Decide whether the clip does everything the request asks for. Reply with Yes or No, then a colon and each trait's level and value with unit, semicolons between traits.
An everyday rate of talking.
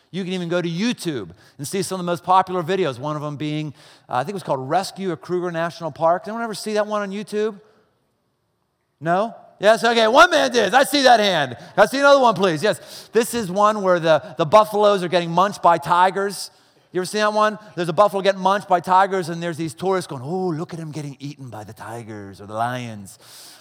No: fast, 240 wpm